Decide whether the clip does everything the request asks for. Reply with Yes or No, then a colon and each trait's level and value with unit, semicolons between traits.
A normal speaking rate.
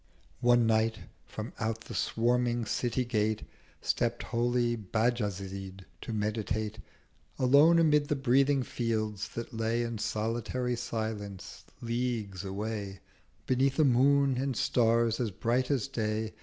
No: slow, 125 wpm